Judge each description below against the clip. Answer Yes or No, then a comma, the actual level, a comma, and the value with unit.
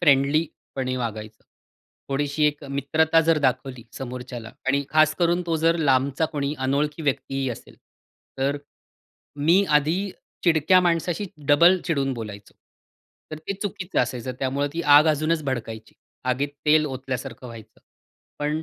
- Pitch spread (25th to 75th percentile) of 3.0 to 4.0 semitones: Yes, average, 3.6 semitones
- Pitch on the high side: No, medium, 140 Hz